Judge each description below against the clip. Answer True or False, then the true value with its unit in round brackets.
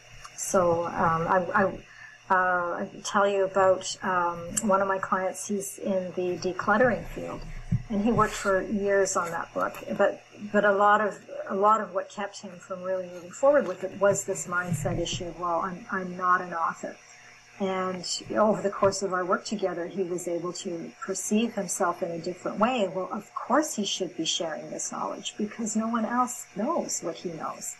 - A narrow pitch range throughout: True (2.3 semitones)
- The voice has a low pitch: False (190 Hz)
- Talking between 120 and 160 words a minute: False (195 wpm)